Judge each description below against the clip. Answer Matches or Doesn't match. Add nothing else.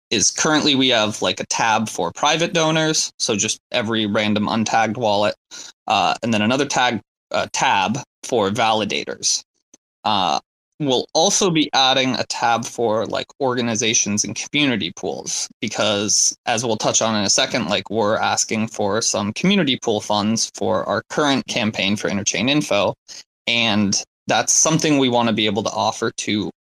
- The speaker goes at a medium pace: Matches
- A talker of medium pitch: Doesn't match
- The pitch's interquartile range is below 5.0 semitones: Doesn't match